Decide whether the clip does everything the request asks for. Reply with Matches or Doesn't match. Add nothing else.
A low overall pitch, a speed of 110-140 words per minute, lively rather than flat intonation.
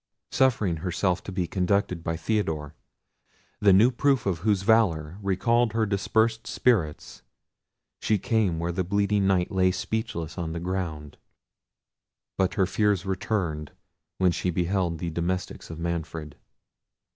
Doesn't match